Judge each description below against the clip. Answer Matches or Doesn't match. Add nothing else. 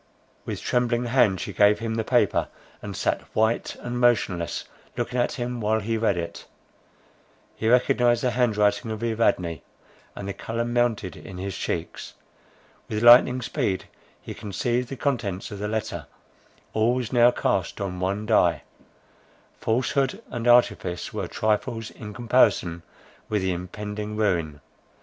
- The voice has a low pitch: Matches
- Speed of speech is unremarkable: Matches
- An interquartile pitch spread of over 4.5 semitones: Doesn't match